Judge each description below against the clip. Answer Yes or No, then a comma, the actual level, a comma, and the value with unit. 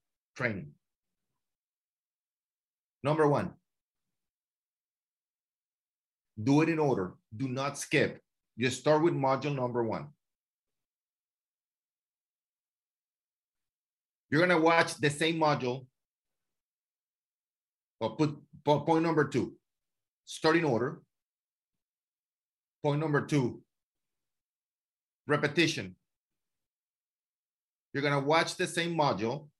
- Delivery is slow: Yes, slow, 80 wpm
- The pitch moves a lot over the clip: No, average, 3.1 semitones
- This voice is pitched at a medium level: Yes, medium, 150 Hz